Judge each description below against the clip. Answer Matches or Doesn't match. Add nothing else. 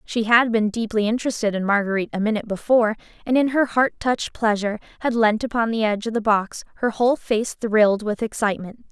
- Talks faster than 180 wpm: Matches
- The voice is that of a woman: Matches